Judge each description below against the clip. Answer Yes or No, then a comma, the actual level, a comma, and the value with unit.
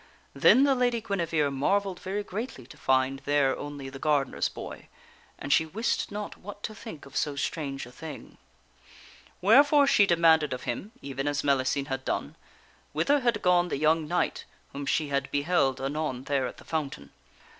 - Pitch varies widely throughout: Yes, wide, 6.4 semitones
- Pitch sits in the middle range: Yes, medium, 150 Hz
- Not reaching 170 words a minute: No, average, 175 wpm